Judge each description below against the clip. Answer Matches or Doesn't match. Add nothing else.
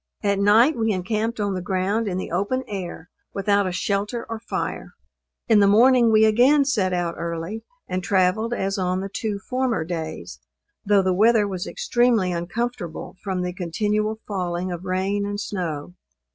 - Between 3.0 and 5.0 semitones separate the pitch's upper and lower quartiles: Matches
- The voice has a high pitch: Matches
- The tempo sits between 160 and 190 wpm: Matches